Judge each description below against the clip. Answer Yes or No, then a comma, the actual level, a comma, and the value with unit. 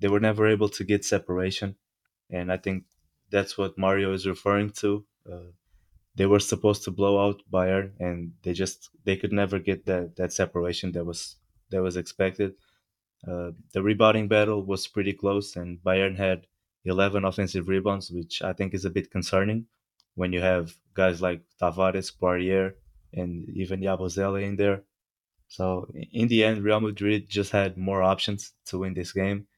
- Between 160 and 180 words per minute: Yes, average, 170 wpm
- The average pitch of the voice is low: Yes, very low, 95 Hz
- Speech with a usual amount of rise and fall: No, narrow, 1.7 semitones